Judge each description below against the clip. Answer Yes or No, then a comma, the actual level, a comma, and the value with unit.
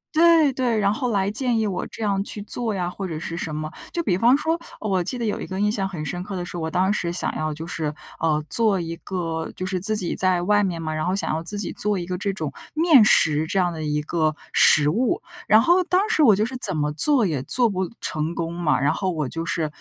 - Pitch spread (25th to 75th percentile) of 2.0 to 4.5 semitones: No, average, 4.9 semitones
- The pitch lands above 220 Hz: No, medium, 185 Hz